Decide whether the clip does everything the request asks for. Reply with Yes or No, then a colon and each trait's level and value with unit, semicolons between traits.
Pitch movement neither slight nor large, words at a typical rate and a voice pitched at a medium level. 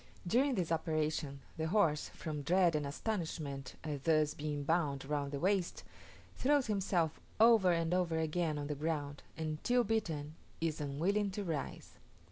Yes: average, 4.0 semitones; average, 155 wpm; medium, 160 Hz